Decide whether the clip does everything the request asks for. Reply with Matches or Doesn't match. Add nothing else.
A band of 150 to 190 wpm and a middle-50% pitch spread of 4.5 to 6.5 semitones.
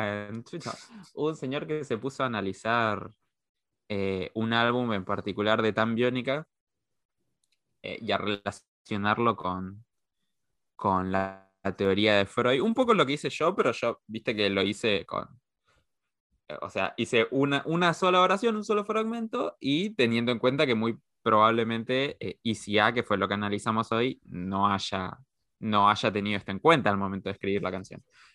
Matches